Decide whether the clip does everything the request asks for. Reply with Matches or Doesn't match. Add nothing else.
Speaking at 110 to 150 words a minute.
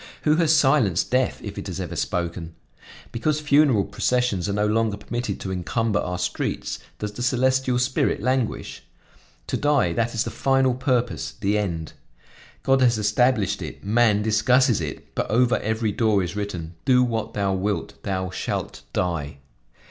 Doesn't match